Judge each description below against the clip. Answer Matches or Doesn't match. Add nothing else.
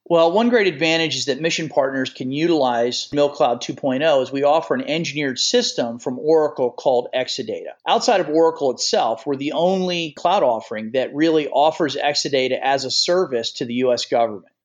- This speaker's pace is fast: Doesn't match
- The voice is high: Doesn't match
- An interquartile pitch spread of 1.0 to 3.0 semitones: Doesn't match